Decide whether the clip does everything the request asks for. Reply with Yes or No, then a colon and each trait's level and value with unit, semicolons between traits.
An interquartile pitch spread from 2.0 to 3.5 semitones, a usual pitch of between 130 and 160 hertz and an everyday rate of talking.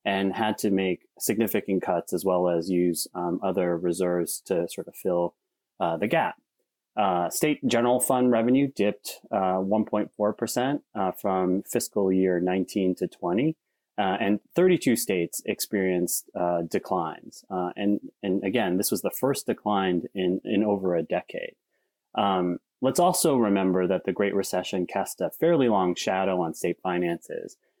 No: average, 3.1 semitones; very low, 95 Hz; average, 155 wpm